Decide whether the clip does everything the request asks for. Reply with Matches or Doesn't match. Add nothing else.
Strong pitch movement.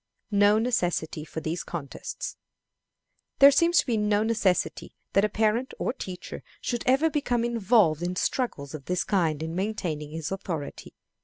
Matches